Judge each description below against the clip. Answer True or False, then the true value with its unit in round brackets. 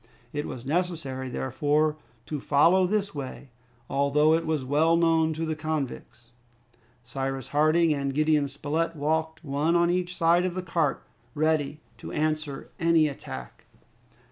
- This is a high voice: False (155 Hz)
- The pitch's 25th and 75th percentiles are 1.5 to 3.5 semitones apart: True (2.7 semitones)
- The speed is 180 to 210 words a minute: False (145 wpm)